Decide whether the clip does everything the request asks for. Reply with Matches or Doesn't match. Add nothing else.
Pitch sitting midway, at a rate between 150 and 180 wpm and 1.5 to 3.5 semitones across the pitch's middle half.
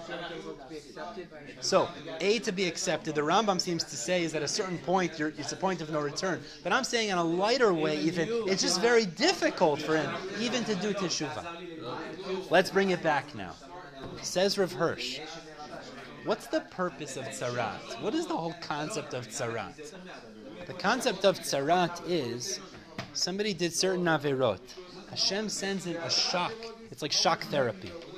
Doesn't match